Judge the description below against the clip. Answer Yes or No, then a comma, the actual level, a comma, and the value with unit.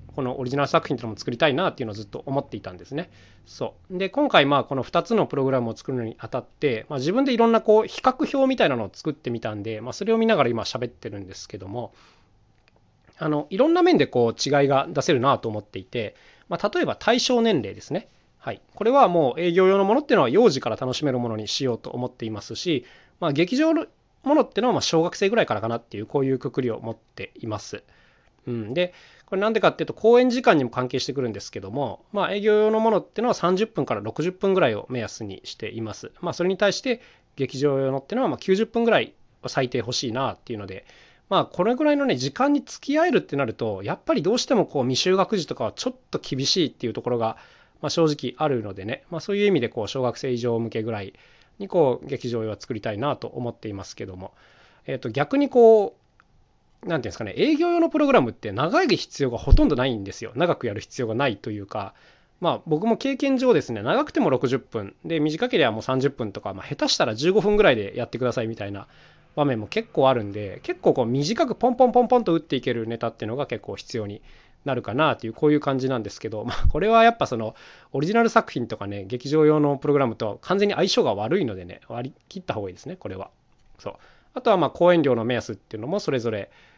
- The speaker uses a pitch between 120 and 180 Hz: Yes, medium, 140 Hz